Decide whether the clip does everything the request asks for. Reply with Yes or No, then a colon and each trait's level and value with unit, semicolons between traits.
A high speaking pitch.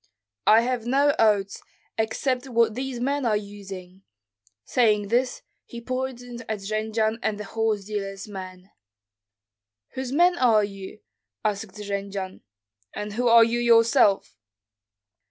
Yes: high, 220 Hz